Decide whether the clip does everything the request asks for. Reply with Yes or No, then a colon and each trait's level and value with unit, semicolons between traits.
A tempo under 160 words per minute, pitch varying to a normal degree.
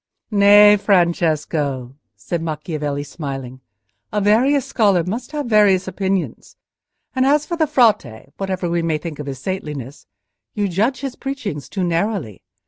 No: average, 140 wpm; wide, 6.0 semitones